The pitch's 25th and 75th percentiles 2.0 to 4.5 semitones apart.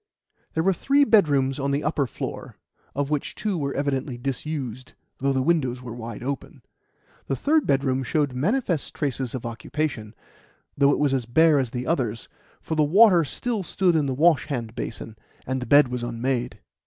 Yes: average, 3.8 semitones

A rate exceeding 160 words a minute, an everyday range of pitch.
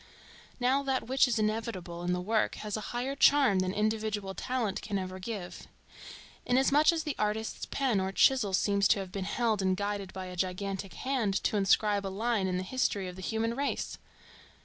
Yes: average, 195 wpm; average, 4.1 semitones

